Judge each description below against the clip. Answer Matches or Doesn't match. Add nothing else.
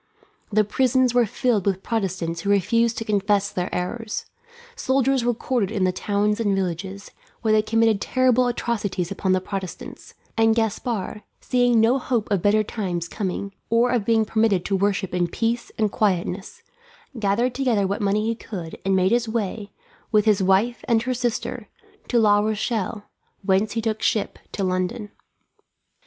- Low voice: Doesn't match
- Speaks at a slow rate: Doesn't match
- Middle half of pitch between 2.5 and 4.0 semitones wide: Matches